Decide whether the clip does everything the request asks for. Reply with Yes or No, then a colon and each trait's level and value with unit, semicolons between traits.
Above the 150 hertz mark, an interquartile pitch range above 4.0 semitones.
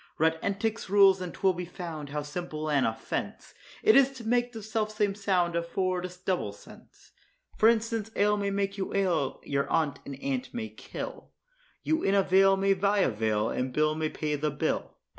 Yes: high, 190 Hz; average, 5.2 semitones